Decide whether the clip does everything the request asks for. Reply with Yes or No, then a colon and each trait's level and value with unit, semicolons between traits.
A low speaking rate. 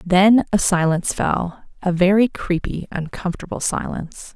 Yes: slow, 125 wpm